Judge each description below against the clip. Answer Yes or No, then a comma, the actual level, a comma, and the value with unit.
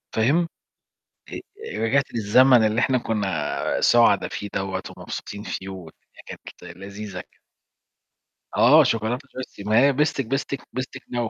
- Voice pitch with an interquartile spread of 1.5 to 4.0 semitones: No, average, 4.4 semitones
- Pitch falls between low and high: No, low, 115 Hz